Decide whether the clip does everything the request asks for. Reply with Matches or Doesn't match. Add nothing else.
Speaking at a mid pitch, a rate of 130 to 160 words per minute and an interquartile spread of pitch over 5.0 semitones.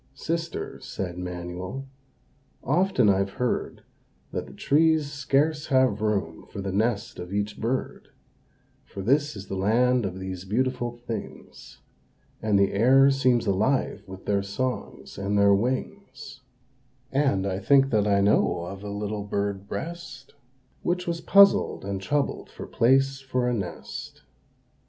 Doesn't match